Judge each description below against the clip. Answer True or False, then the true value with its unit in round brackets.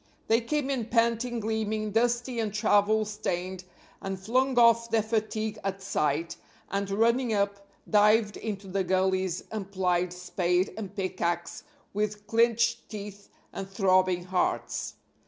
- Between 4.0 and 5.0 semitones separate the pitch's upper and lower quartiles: False (3.1 semitones)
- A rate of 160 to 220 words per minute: False (135 wpm)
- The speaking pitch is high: True (205 Hz)